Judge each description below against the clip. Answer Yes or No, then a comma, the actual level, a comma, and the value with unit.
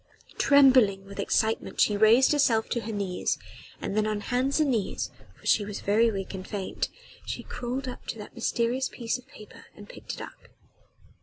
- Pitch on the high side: Yes, high, 225 Hz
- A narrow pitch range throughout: No, average, 3.7 semitones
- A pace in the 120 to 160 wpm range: No, average, 185 wpm